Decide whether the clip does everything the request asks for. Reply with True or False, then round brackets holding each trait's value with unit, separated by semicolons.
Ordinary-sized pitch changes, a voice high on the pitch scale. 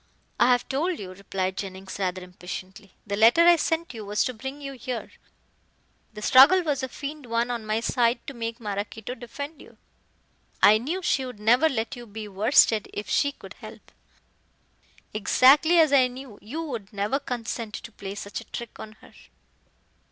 True (4.8 semitones; 235 Hz)